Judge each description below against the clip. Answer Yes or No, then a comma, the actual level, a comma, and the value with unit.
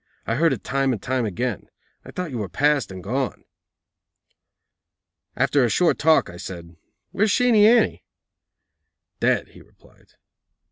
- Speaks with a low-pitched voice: Yes, low, 130 Hz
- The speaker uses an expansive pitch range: Yes, wide, 7.2 semitones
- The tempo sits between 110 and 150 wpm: Yes, average, 145 wpm